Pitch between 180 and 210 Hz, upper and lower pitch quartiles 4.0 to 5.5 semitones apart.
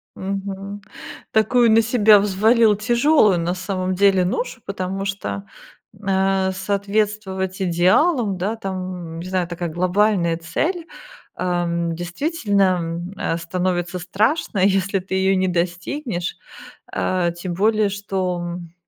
No: high, 190 Hz; narrow, 2.6 semitones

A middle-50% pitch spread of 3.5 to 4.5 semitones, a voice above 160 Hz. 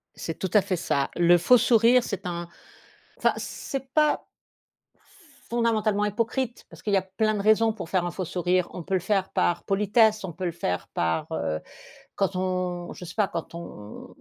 Yes: average, 3.8 semitones; high, 190 Hz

